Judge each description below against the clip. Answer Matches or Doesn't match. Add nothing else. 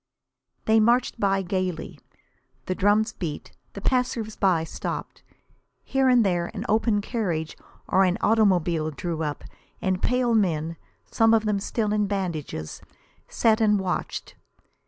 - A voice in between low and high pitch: Doesn't match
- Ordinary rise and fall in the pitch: Matches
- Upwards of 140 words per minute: Doesn't match